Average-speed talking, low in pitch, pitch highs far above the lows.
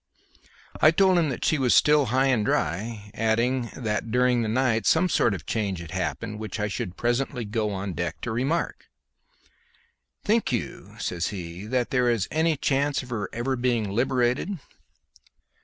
No: average, 170 wpm; low, 120 Hz; average, 4.1 semitones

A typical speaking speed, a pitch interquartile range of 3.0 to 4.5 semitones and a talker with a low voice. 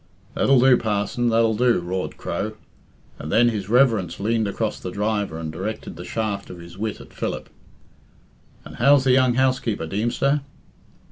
Yes: average, 160 wpm; average, 3.6 semitones; low, 110 Hz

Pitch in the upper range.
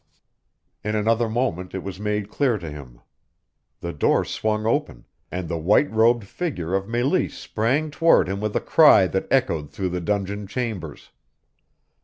No: low, 105 Hz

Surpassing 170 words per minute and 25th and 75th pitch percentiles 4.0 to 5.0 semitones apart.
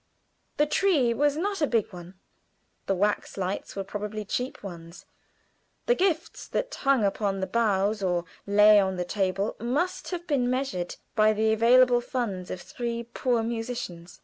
No: average, 160 wpm; average, 4.7 semitones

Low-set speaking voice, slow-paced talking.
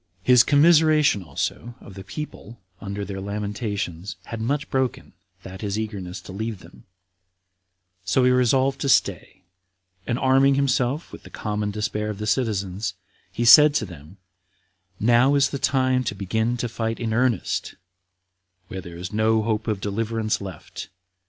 No: low, 110 Hz; average, 155 wpm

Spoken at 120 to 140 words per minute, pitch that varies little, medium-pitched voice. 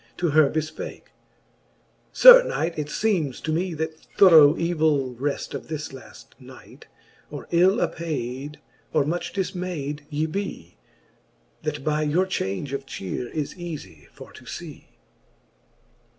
No: slow, 135 wpm; average, 3.5 semitones; medium, 155 Hz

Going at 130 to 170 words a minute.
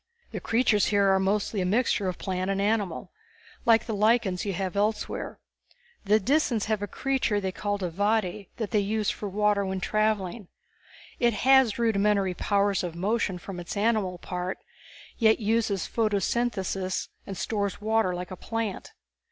Yes: average, 160 wpm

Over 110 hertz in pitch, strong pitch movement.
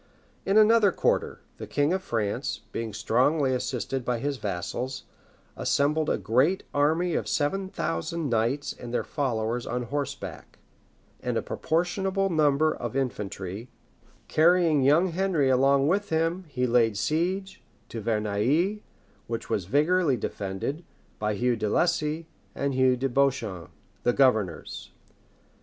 Yes: low, 135 Hz; wide, 5.8 semitones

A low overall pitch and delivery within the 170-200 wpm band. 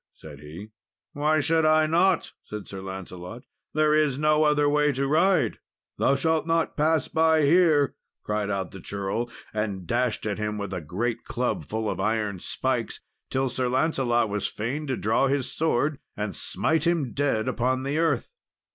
Yes: low, 130 Hz; average, 175 wpm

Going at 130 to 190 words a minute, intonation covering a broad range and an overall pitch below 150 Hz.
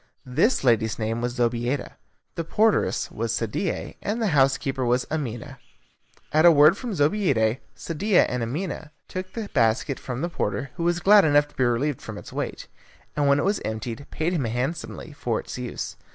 Yes: average, 180 wpm; wide, 5.9 semitones; medium, 140 Hz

